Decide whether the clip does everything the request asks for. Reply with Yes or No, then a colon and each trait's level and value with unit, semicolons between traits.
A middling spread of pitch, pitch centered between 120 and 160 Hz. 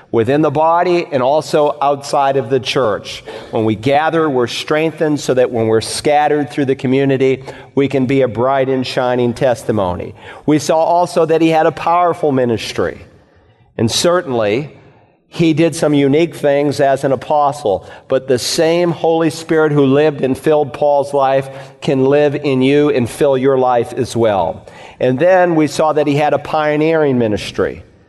Yes: average, 3.0 semitones; medium, 140 Hz